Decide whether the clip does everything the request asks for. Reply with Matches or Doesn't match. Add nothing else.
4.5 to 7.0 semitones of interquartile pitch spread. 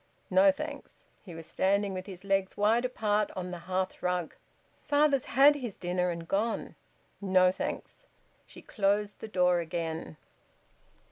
Doesn't match